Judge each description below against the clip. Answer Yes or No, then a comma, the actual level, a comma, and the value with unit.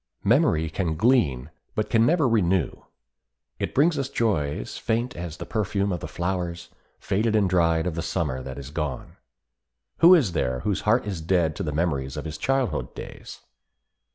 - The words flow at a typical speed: Yes, average, 175 wpm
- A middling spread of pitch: No, wide, 5.8 semitones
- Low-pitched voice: Yes, very low, 90 Hz